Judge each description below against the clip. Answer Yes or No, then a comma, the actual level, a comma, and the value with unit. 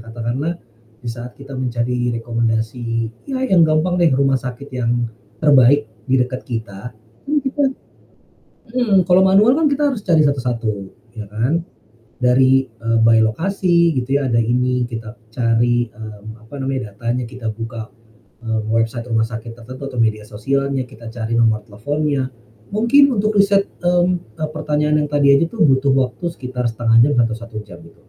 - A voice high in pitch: No, low, 125 Hz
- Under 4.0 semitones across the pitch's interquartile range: No, average, 4.8 semitones